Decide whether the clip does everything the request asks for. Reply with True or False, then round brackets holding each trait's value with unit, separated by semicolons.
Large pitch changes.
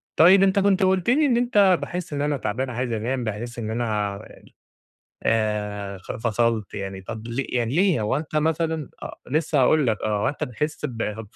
True (6.9 semitones)